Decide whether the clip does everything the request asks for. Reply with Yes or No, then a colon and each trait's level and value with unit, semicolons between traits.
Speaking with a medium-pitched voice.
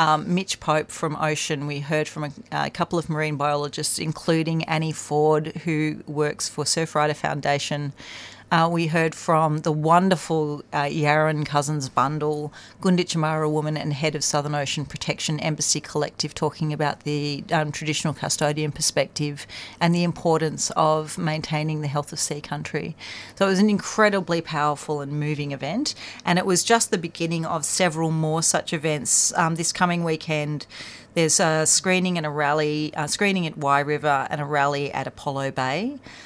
Yes: medium, 155 Hz